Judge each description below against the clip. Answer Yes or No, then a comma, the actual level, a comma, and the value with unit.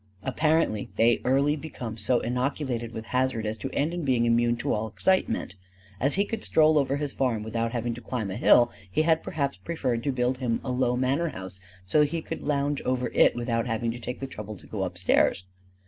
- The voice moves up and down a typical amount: Yes, average, 3.6 semitones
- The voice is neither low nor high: No, low, 125 Hz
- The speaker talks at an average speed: No, fast, 215 wpm